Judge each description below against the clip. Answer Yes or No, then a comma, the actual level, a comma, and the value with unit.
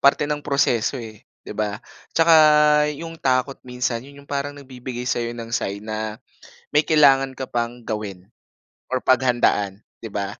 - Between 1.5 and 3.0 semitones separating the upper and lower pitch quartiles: No, average, 4.2 semitones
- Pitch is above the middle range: No, low, 125 Hz